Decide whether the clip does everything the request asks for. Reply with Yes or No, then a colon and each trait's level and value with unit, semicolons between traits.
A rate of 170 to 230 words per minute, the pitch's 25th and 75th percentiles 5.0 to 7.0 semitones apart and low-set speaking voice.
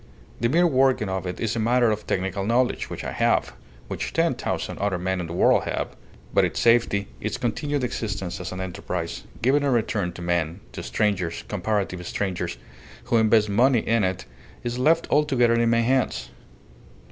No: average, 180 wpm; average, 4.5 semitones; low, 110 Hz